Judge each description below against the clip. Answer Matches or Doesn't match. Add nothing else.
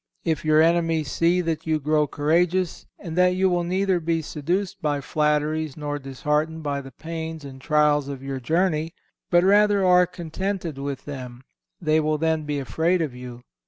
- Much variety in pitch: Doesn't match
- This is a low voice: Doesn't match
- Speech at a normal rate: Matches